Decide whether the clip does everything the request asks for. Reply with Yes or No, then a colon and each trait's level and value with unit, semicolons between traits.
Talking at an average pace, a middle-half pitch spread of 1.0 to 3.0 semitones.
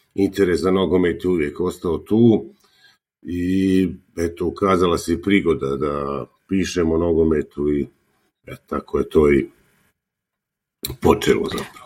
Yes: average, 120 wpm; average, 2.7 semitones